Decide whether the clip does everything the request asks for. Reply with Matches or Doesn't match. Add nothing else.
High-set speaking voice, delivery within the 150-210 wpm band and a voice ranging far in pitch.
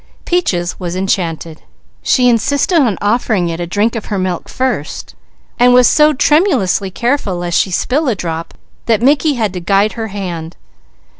Matches